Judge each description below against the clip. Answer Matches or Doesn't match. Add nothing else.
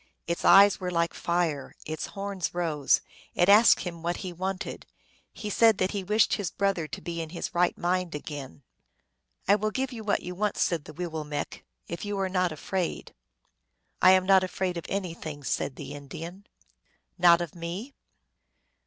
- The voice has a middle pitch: Matches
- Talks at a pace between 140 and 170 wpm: Doesn't match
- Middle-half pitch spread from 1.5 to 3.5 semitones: Matches